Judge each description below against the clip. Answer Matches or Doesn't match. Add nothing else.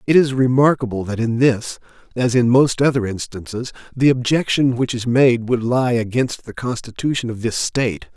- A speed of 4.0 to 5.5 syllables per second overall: Matches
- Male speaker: Matches